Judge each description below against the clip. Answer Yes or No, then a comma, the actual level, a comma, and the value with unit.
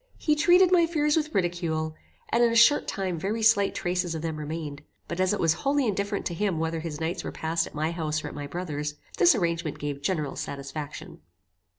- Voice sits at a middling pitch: Yes, medium, 170 Hz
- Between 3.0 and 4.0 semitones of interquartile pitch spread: No, average, 4.9 semitones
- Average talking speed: No, fast, 215 wpm